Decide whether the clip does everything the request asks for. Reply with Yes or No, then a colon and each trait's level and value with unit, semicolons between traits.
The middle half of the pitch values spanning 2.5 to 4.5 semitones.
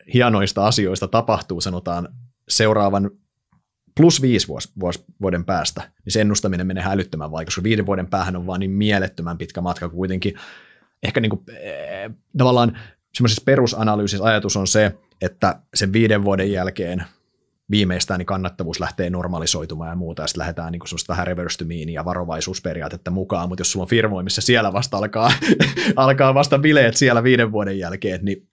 Yes: average, 3.5 semitones